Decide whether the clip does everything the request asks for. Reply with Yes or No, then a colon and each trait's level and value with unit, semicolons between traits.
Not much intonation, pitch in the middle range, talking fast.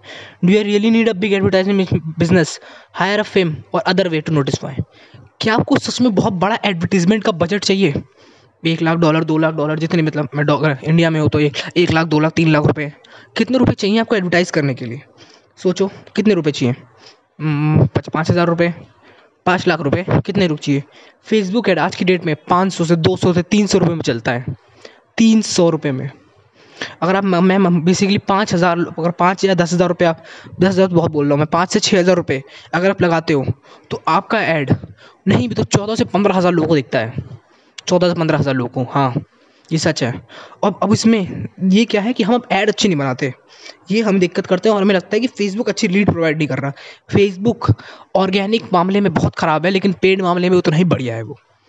No: average, 4.6 semitones; medium, 175 Hz; fast, 215 wpm